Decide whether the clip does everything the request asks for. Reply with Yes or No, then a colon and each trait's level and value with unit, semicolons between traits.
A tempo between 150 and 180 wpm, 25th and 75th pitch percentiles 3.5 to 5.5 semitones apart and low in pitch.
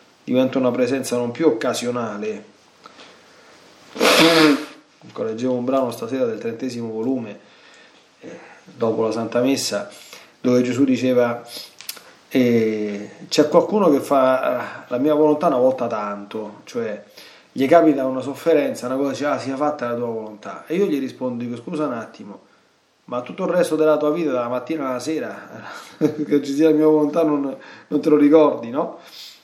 Yes: average, 160 wpm; average, 4.0 semitones; low, 130 Hz